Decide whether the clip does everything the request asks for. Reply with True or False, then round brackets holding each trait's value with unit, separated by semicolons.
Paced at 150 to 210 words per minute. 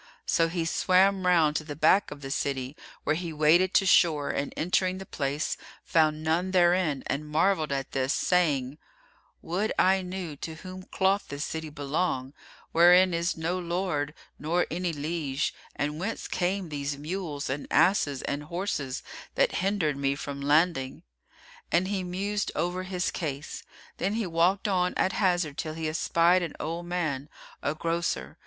True (160 wpm)